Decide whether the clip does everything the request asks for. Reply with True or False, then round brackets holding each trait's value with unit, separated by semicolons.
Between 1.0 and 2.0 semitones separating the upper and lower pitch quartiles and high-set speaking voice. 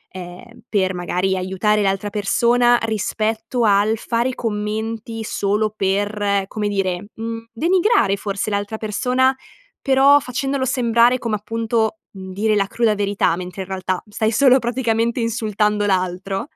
False (2.8 semitones; 215 Hz)